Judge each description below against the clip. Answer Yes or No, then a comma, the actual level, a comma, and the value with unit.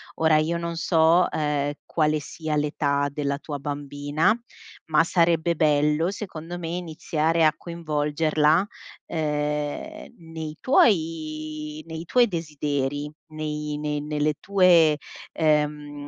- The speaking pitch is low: No, medium, 155 Hz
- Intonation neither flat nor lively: No, narrow, 1.8 semitones